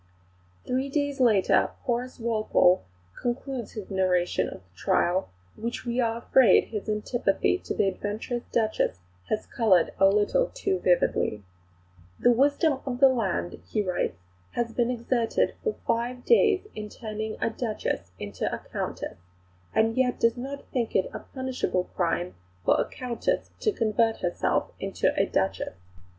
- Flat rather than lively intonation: No, average, 4.6 semitones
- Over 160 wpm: No, average, 150 wpm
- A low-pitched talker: No, high, 230 Hz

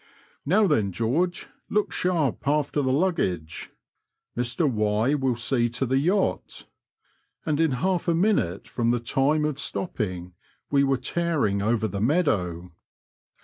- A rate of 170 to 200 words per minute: No, average, 145 wpm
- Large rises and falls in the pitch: Yes, wide, 7.0 semitones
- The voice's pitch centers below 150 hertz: Yes, low, 135 Hz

